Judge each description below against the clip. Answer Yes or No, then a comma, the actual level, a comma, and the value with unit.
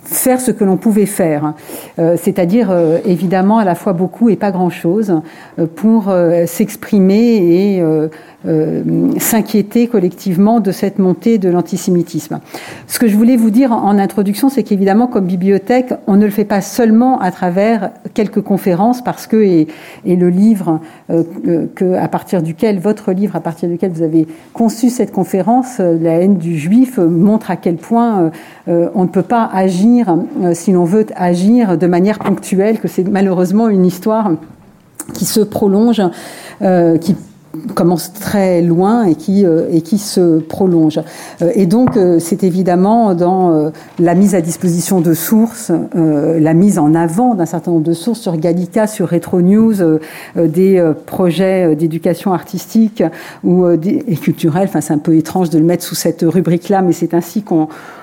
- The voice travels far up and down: No, average, 3.7 semitones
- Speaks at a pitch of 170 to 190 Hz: Yes, medium, 185 Hz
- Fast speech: No, average, 165 wpm